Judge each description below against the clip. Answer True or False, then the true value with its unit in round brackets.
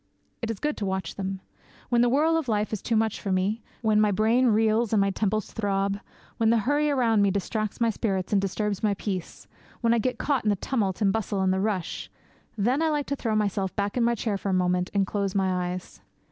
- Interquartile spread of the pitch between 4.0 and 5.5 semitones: False (2.9 semitones)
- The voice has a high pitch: True (210 Hz)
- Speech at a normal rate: False (245 wpm)